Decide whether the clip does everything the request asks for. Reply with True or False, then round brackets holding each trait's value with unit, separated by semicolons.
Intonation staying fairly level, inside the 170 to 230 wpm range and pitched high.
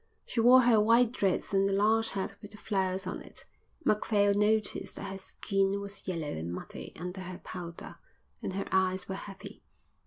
True (2.1 semitones; 185 wpm; 195 Hz)